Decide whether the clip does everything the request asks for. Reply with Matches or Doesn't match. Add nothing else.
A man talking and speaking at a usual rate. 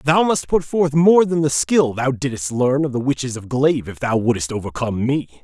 Doesn't match